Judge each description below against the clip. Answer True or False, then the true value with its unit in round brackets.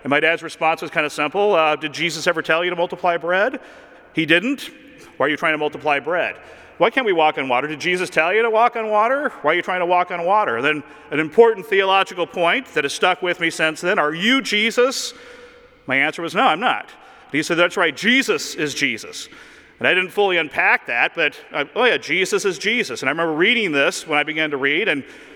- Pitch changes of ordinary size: False (6.2 semitones)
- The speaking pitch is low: False (175 Hz)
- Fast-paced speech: True (240 wpm)